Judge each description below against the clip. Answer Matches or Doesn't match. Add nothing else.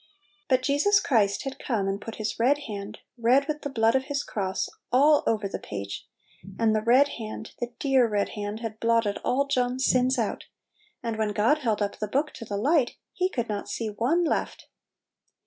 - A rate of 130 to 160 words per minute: Doesn't match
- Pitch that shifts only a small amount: Doesn't match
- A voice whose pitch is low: Doesn't match